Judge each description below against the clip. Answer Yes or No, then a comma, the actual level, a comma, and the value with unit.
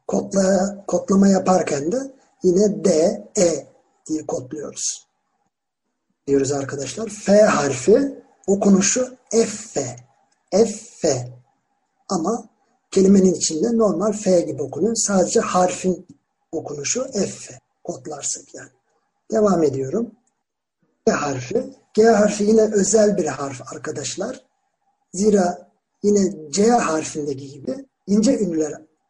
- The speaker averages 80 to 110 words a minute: Yes, average, 105 wpm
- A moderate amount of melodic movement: No, wide, 6.0 semitones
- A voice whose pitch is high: Yes, high, 195 Hz